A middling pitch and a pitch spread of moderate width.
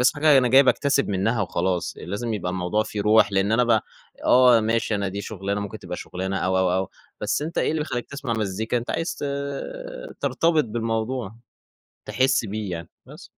No: low, 110 Hz; average, 4.4 semitones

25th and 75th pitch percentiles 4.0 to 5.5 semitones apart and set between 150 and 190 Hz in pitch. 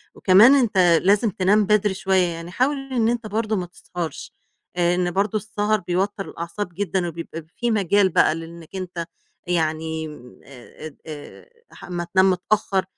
No: average, 3.5 semitones; medium, 185 Hz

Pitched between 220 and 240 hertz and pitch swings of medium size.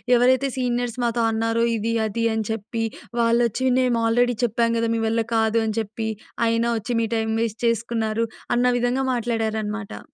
No: high, 230 Hz; narrow, 1.4 semitones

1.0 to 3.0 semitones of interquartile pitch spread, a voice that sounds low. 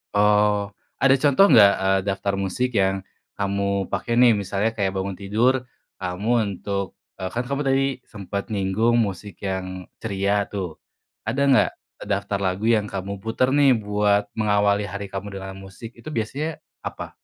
Yes: narrow, 2.6 semitones; low, 100 Hz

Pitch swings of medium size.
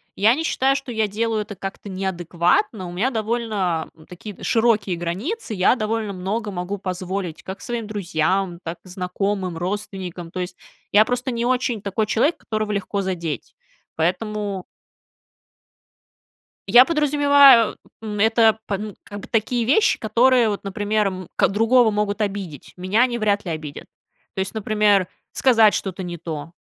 Yes: average, 3.5 semitones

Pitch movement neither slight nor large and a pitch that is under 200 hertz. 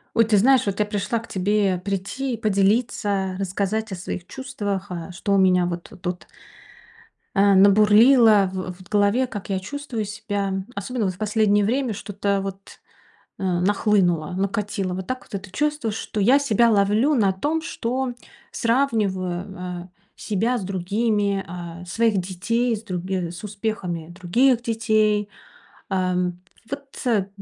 No: average, 3.2 semitones; high, 205 Hz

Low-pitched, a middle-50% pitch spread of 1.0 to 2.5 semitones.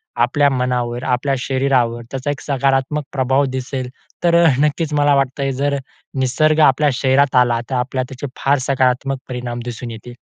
Yes: low, 130 Hz; narrow, 2.2 semitones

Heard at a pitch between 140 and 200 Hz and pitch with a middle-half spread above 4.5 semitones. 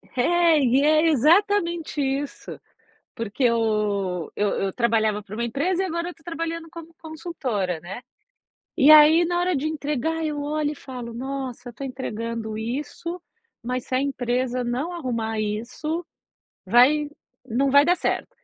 No: very high, 270 Hz; wide, 5.5 semitones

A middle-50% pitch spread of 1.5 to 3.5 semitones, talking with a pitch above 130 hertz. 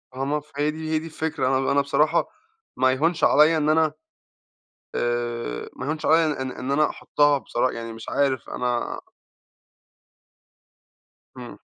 Yes: average, 3.1 semitones; medium, 140 Hz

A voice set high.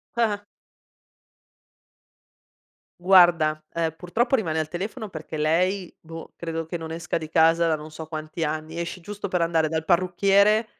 No: medium, 165 Hz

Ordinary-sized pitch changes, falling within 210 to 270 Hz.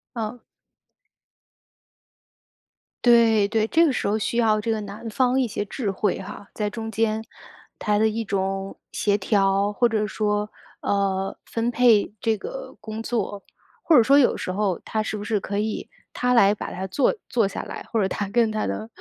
No: narrow, 2.2 semitones; high, 215 Hz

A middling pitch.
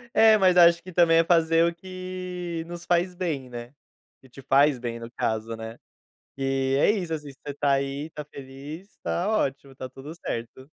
Yes: medium, 150 Hz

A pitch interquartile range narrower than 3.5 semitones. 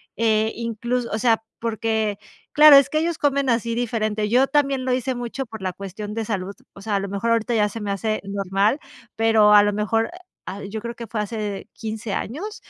Yes: narrow, 2.6 semitones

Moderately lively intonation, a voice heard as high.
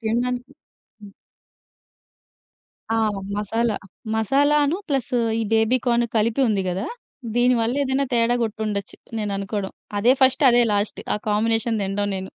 Yes: average, 3.0 semitones; high, 225 Hz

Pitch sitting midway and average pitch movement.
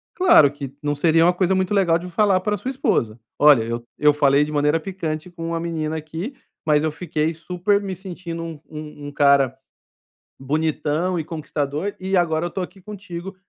Yes: medium, 165 Hz; average, 3.7 semitones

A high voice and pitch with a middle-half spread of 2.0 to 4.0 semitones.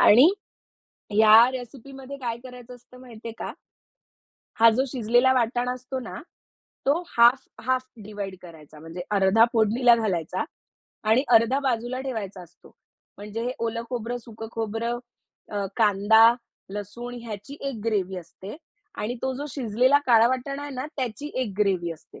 Yes: high, 230 Hz; average, 3.3 semitones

